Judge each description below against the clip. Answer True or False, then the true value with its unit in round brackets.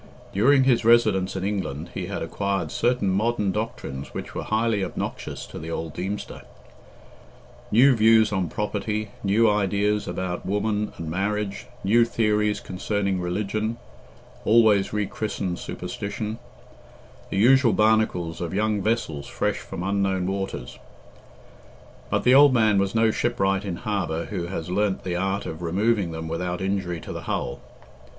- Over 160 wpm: False (145 wpm)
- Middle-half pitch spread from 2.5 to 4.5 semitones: True (2.8 semitones)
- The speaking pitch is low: True (100 Hz)